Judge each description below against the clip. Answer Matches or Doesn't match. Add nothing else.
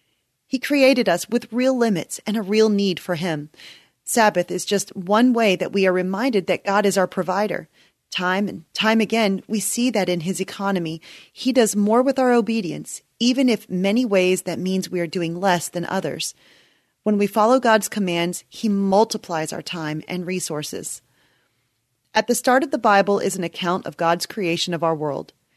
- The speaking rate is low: Doesn't match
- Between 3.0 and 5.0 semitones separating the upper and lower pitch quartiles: Matches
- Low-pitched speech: Doesn't match